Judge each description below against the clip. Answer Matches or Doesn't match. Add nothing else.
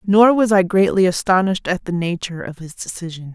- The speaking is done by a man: Doesn't match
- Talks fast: Doesn't match